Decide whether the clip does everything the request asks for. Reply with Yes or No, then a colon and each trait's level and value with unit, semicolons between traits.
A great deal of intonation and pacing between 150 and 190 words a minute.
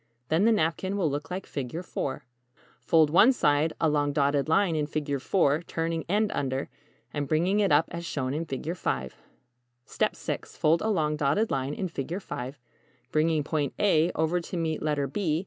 No: average, 3.3 semitones; average, 180 wpm